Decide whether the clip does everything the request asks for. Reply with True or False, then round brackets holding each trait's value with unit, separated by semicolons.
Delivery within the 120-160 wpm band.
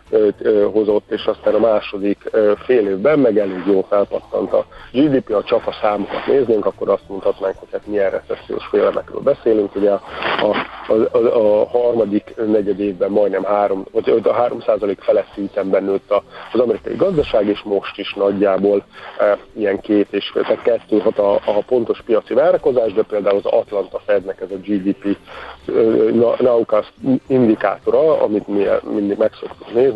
True (150 wpm)